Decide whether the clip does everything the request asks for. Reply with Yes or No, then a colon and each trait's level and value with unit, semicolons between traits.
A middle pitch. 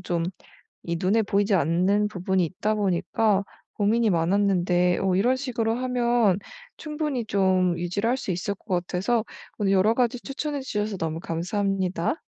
No: high, 200 Hz